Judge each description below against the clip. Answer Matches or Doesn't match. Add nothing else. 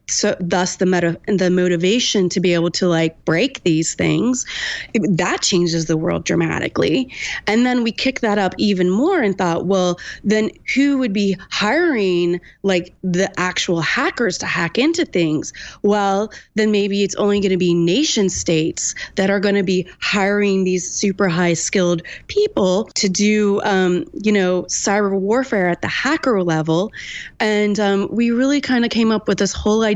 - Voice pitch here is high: Matches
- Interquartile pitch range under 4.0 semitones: Matches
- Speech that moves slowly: Doesn't match